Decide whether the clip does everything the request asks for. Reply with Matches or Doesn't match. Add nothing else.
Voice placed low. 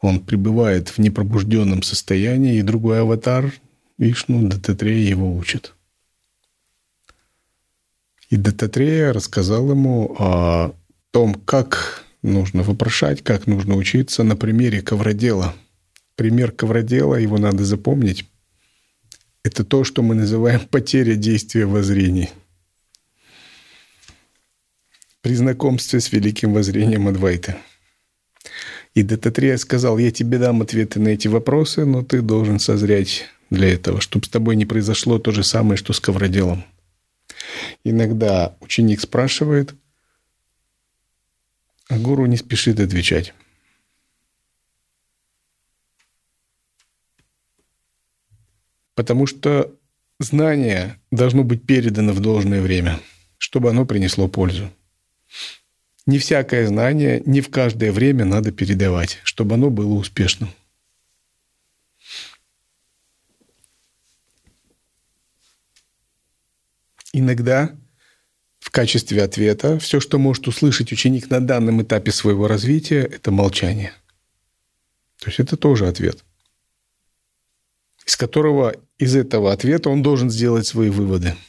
Matches